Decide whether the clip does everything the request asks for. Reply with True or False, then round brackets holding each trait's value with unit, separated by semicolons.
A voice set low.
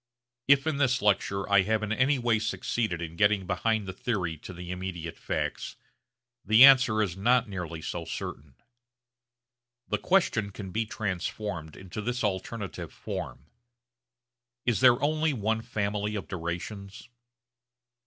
True (105 Hz)